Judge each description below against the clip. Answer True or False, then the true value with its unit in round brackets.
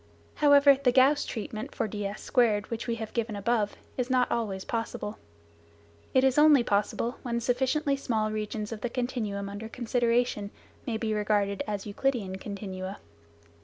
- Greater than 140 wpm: True (150 wpm)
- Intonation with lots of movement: False (3.2 semitones)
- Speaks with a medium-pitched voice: False (225 Hz)